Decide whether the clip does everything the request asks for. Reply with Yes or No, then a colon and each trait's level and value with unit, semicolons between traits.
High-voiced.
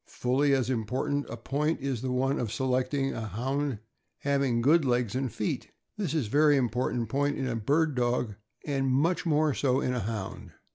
No: low, 130 Hz